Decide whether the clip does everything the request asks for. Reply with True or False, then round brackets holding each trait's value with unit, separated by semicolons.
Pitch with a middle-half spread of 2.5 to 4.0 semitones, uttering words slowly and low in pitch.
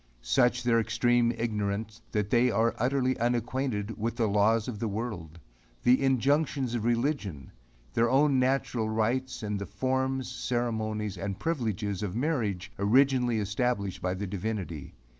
False (3.5 semitones; 145 wpm; 115 Hz)